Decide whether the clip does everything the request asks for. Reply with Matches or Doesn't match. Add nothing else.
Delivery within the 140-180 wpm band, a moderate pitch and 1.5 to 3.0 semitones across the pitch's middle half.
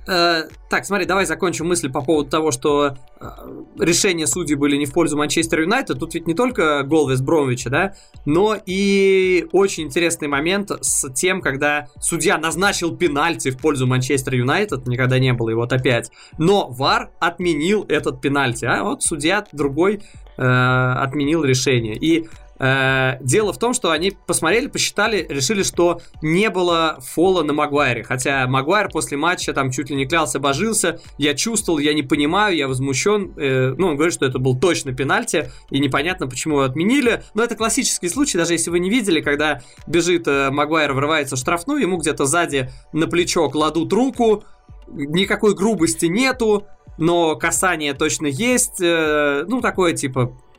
Doesn't match